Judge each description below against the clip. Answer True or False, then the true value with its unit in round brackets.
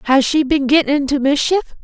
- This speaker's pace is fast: False (195 wpm)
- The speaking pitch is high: True (285 Hz)